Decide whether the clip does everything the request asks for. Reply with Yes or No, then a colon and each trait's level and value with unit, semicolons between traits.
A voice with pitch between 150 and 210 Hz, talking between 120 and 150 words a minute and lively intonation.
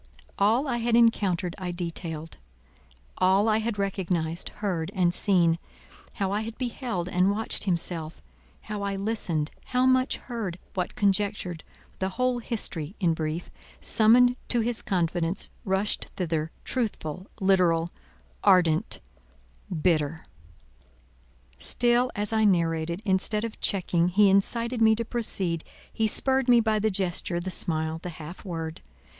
No: high, 190 Hz; slow, 135 wpm; average, 4.5 semitones